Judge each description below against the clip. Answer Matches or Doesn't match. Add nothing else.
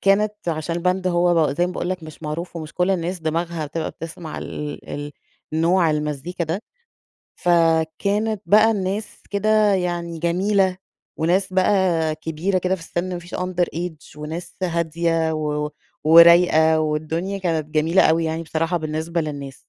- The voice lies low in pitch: Doesn't match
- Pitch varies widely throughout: Doesn't match